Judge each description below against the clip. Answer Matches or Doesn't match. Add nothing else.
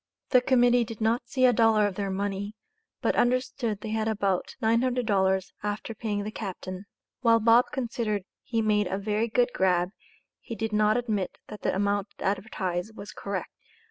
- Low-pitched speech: Doesn't match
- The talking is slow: Doesn't match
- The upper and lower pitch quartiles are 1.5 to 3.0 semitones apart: Matches